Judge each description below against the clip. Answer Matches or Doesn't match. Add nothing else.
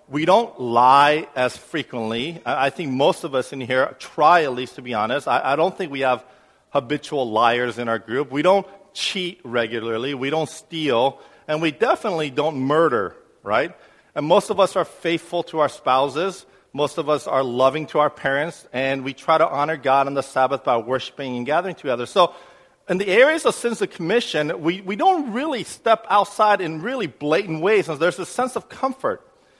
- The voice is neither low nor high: Matches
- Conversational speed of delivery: Matches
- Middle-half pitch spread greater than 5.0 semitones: Matches